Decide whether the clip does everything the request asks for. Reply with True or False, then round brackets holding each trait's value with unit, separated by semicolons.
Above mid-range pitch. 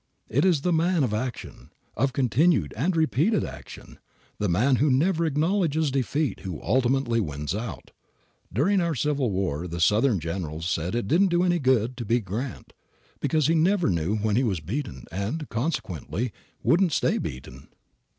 False (130 Hz)